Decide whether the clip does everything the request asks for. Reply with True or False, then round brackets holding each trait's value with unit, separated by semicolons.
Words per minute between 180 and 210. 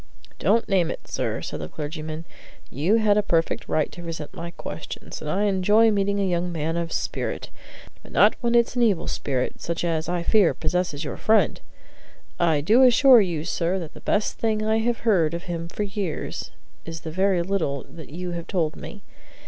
True (195 wpm)